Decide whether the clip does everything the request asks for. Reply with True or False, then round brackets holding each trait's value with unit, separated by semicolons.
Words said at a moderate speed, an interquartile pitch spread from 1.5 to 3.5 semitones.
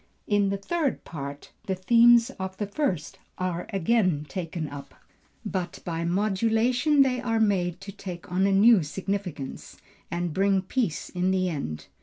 False (155 wpm; 4.2 semitones)